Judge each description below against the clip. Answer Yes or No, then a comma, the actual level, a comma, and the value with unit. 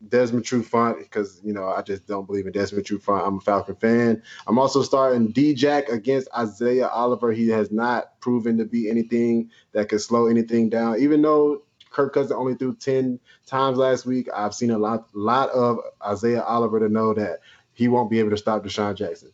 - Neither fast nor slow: No, fast, 210 wpm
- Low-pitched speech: Yes, low, 115 Hz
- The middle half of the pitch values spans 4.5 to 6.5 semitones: No, average, 2.8 semitones